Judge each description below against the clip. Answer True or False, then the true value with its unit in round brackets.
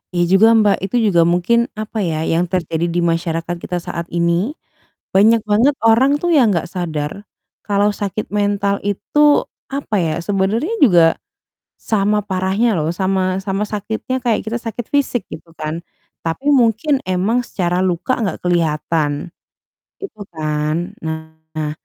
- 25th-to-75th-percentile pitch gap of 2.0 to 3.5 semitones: False (4.8 semitones)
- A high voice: True (195 Hz)